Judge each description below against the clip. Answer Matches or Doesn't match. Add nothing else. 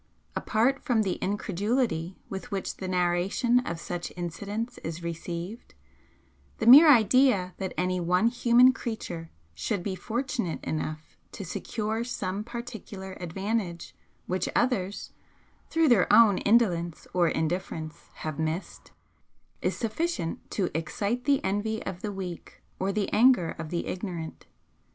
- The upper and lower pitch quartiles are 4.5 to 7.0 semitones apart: Matches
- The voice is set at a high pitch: Matches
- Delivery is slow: Matches